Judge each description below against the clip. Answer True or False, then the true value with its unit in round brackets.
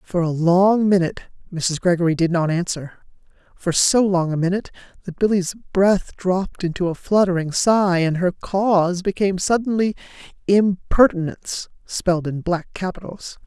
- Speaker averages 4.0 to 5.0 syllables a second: True (4.9 syllables/s)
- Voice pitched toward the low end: False (185 Hz)